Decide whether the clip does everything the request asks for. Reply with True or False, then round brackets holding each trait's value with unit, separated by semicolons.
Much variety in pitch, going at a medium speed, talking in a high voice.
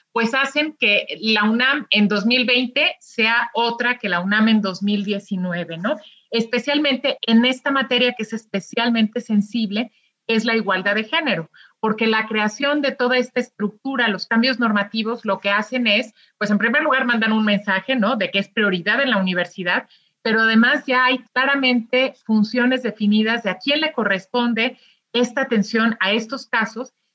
False (3.3 semitones; 165 wpm; 230 Hz)